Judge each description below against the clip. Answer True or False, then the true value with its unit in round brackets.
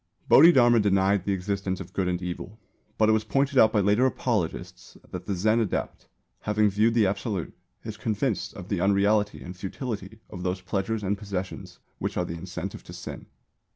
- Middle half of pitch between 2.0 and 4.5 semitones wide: True (2.6 semitones)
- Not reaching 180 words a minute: False (185 wpm)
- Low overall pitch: True (100 Hz)